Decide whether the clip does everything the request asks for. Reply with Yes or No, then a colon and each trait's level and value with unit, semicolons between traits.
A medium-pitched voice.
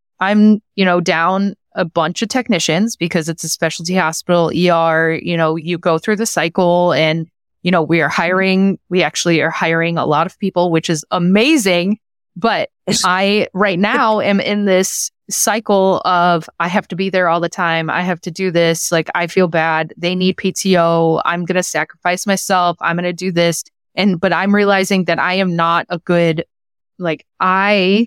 Yes: medium, 180 Hz